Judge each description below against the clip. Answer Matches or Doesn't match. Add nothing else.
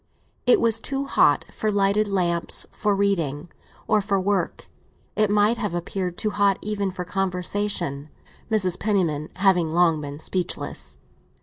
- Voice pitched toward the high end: Matches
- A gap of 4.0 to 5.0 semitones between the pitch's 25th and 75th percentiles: Doesn't match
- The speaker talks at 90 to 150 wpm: Matches